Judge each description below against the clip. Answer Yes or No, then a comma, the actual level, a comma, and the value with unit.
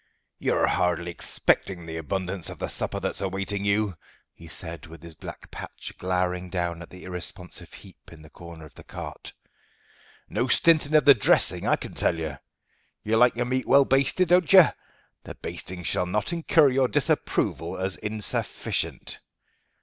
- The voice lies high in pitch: No, very low, 95 Hz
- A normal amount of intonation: No, wide, 6.5 semitones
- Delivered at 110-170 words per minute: Yes, average, 165 wpm